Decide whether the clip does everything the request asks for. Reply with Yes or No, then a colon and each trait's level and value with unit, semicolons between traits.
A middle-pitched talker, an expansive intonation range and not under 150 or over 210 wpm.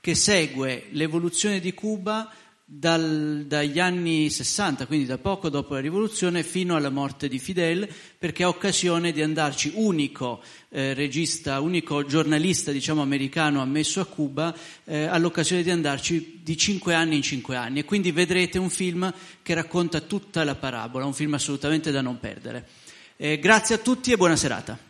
No: medium, 160 Hz; average, 3.7 semitones; average, 165 wpm